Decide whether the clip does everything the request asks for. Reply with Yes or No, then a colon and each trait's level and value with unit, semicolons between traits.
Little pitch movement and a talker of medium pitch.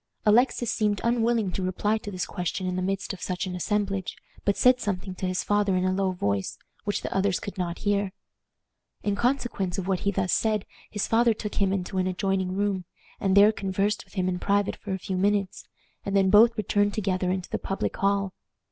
No: narrow, 1.9 semitones; high, 195 Hz